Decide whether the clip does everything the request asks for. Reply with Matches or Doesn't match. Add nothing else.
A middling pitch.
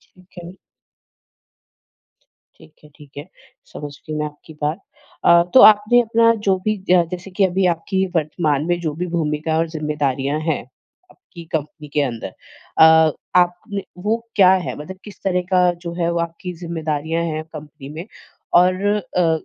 Matches